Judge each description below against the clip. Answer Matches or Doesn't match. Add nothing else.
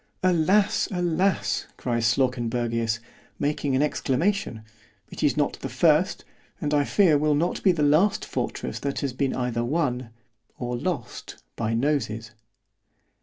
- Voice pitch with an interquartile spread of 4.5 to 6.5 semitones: Matches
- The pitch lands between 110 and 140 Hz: Matches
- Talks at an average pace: Doesn't match